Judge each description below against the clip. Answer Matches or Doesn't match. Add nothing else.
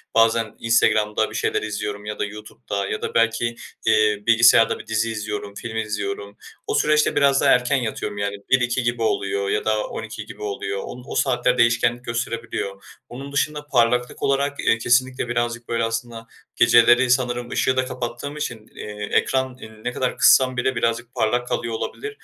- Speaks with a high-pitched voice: Doesn't match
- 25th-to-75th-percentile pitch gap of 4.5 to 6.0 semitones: Doesn't match